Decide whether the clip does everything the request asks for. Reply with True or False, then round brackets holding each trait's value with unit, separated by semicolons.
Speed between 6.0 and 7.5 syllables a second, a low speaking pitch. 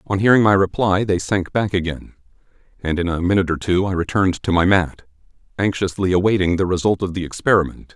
True (6.2 syllables/s; 95 Hz)